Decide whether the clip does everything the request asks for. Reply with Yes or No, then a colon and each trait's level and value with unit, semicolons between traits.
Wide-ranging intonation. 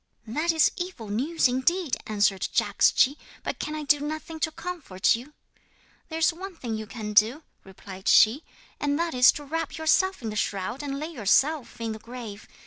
Yes: wide, 6.5 semitones